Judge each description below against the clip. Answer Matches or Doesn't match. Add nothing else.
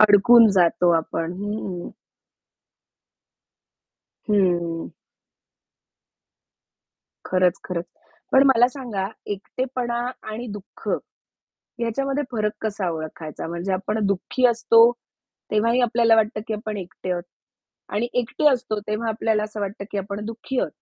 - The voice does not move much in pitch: Doesn't match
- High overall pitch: Matches